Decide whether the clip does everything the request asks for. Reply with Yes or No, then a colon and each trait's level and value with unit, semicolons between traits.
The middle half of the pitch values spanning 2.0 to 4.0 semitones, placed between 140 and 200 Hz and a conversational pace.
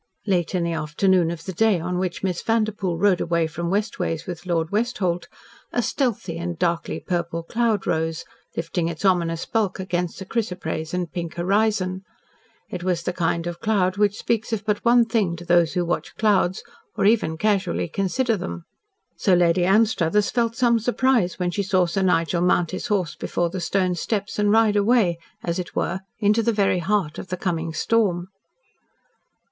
Yes: average, 3.5 semitones; medium, 185 Hz; average, 185 wpm